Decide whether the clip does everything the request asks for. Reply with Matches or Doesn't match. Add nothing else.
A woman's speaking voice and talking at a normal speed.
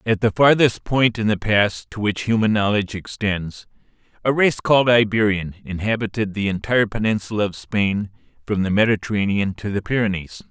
Doesn't match